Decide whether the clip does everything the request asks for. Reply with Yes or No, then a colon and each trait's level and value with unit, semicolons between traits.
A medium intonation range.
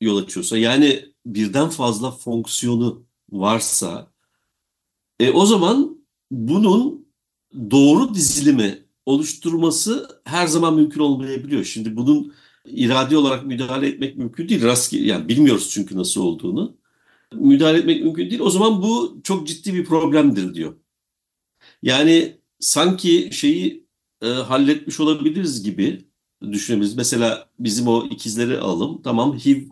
No: wide, 7.3 semitones